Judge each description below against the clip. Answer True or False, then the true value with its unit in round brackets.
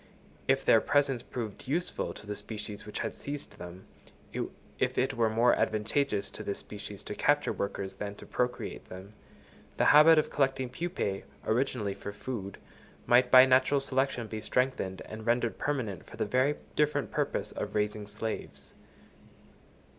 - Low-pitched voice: True (115 Hz)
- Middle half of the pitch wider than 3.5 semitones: True (4.3 semitones)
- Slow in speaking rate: False (150 wpm)